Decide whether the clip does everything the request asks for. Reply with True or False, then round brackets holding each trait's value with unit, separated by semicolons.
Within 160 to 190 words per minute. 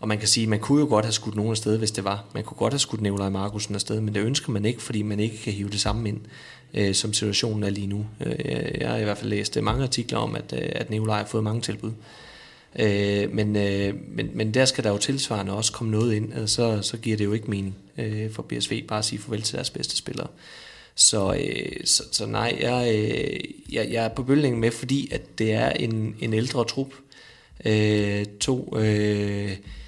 False (215 wpm)